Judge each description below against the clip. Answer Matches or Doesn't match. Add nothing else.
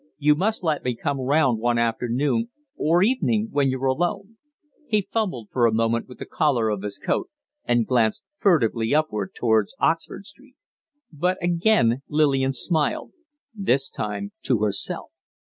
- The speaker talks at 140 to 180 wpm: Matches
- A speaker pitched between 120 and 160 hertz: Matches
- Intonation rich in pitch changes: Matches